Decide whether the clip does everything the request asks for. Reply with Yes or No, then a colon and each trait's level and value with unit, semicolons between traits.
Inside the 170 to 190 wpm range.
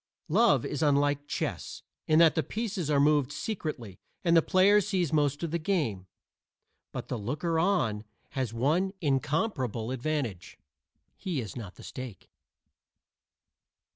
No: average, 140 wpm